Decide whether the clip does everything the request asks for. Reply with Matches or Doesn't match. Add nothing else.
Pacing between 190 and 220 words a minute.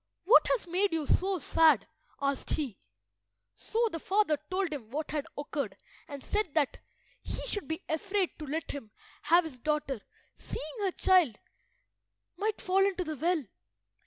Doesn't match